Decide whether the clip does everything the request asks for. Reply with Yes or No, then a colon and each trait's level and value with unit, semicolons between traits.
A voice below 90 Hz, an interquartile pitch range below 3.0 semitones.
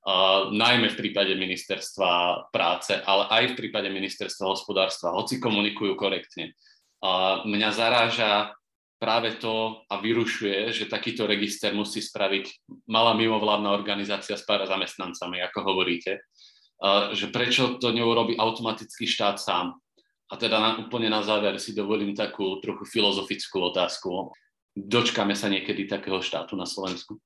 No: low, 105 Hz; narrow, 2.4 semitones